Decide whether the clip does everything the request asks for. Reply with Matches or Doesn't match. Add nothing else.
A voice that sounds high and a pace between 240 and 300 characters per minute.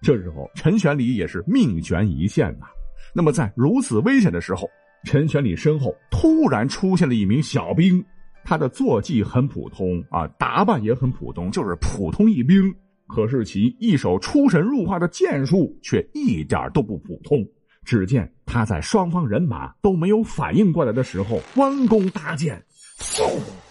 Doesn't match